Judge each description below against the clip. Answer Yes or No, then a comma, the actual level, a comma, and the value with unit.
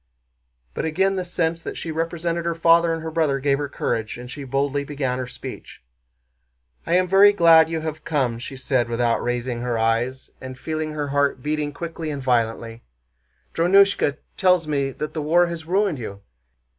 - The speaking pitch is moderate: Yes, medium, 150 Hz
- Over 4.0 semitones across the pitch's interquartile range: Yes, average, 4.4 semitones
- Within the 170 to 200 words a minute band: Yes, average, 180 wpm